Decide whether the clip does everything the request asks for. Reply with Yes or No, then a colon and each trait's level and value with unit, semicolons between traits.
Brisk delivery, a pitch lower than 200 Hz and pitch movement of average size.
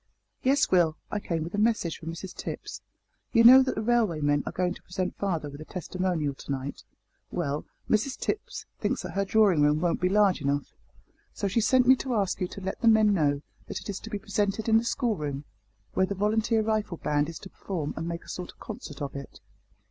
No: fast, 225 wpm; medium, 185 Hz; wide, 5.7 semitones